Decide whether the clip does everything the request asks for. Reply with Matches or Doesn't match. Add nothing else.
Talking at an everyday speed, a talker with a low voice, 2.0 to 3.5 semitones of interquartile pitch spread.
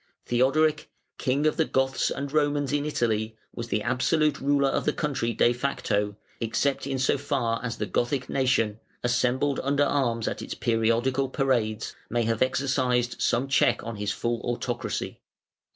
Matches